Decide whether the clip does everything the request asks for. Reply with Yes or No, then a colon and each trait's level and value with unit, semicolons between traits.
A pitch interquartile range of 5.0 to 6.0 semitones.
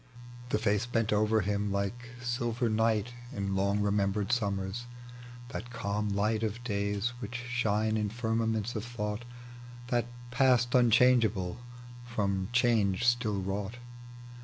No: average, 2.9 semitones